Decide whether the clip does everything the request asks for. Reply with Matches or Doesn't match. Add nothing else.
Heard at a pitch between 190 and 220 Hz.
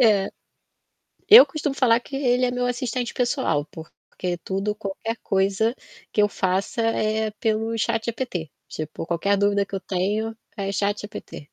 Matches